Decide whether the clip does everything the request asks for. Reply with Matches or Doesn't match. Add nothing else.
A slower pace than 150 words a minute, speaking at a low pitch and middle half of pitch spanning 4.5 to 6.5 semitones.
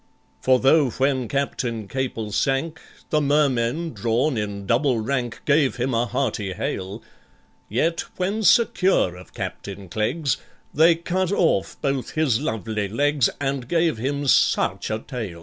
Matches